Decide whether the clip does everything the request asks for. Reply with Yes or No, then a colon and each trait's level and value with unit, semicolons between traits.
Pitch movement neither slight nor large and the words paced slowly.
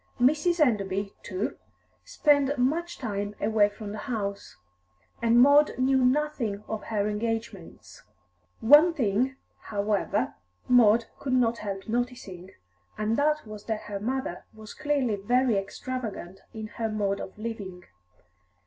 Yes: average, 4.1 semitones; slow, 130 wpm